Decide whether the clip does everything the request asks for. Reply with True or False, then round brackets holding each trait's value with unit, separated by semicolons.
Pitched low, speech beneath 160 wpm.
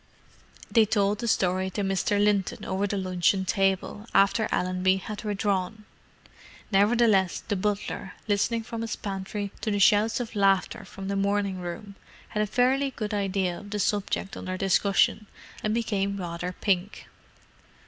False (200 Hz; 150 wpm)